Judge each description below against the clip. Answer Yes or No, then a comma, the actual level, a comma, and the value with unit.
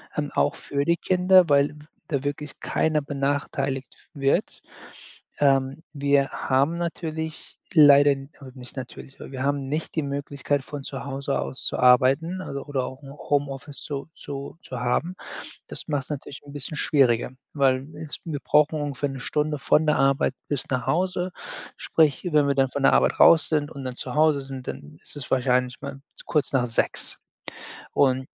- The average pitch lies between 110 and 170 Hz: Yes, medium, 140 Hz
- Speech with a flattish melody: Yes, narrow, 1.9 semitones